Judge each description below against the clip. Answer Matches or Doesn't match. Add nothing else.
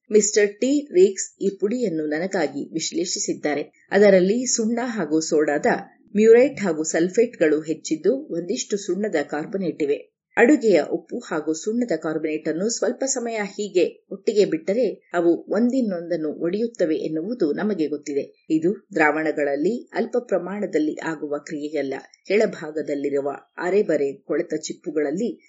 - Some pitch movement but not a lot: Doesn't match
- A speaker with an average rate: Doesn't match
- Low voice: Doesn't match